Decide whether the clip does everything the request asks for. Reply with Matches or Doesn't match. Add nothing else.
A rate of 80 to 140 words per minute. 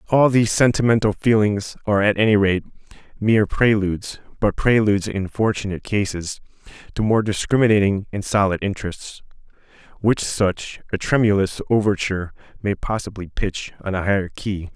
Matches